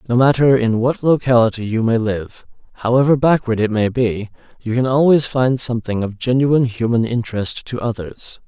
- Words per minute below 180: Yes, average, 170 wpm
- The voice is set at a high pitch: No, low, 120 Hz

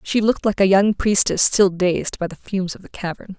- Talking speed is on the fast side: Yes, fast, 250 wpm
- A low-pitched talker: No, high, 195 Hz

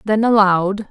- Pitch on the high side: Yes, high, 205 Hz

